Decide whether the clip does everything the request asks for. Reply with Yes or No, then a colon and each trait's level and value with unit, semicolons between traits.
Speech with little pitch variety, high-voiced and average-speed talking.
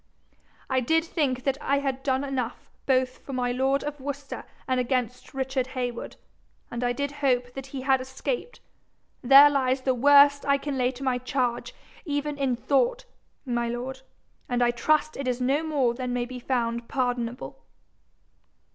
Yes: narrow, 2.2 semitones; very high, 260 Hz; average, 170 wpm